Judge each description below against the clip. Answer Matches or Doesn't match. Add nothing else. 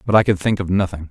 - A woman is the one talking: Doesn't match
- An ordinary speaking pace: Doesn't match